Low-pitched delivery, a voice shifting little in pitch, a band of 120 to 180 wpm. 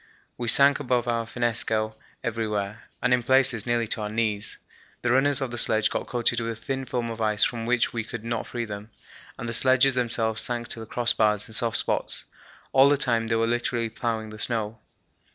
No: low, 115 Hz; narrow, 1.7 semitones; fast, 205 wpm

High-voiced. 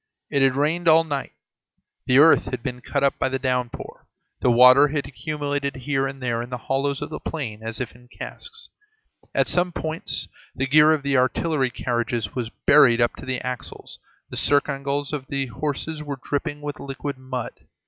No: low, 135 Hz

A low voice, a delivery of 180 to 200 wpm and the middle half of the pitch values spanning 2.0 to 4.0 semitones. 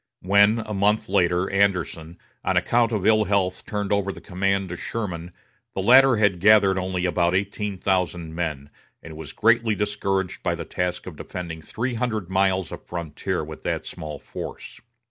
No: very low, 95 Hz; average, 170 wpm; average, 2.8 semitones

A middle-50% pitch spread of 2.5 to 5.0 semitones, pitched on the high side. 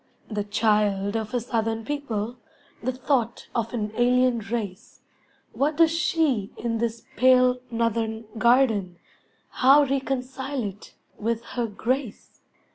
Yes: average, 2.9 semitones; high, 235 Hz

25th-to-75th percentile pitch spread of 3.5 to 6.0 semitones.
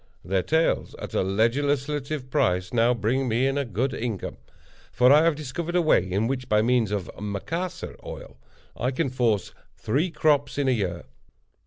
Yes: average, 5.2 semitones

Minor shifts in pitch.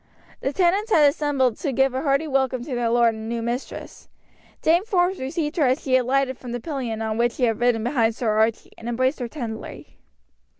No: average, 3.6 semitones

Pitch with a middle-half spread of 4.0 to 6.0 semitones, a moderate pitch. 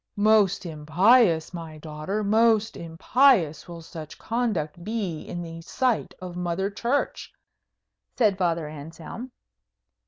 Yes: average, 5.2 semitones; medium, 180 Hz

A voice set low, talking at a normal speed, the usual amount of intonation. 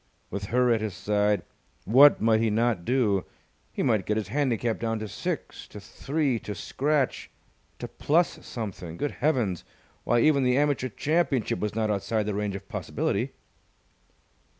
Yes: low, 115 Hz; average, 160 wpm; average, 4.2 semitones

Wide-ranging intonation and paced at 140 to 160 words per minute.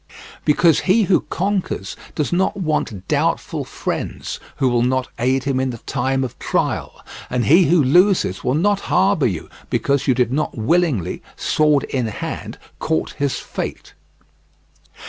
Yes: wide, 5.7 semitones; average, 150 wpm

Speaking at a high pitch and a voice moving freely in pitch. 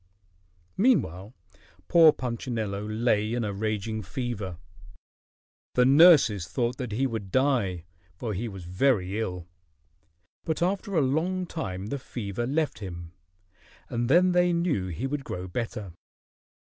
No: low, 115 Hz; wide, 6.2 semitones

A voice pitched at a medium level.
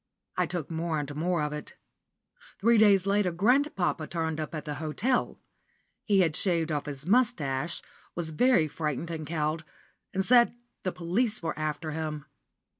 Yes: medium, 165 Hz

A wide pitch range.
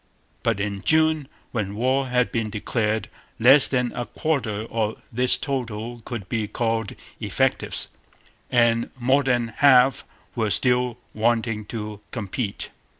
No: average, 2.7 semitones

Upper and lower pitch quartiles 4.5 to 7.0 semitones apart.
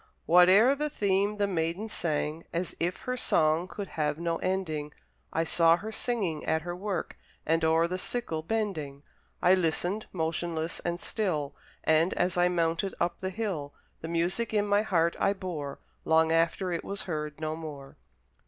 No: average, 3.3 semitones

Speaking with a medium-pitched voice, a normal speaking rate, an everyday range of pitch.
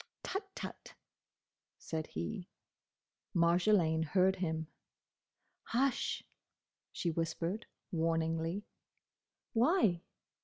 No: medium, 170 Hz; slow, 70 wpm; average, 4.0 semitones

